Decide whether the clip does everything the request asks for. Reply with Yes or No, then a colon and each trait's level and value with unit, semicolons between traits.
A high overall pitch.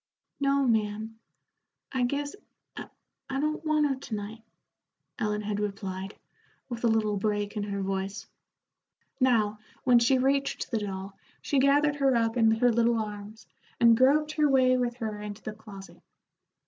Yes: high, 225 Hz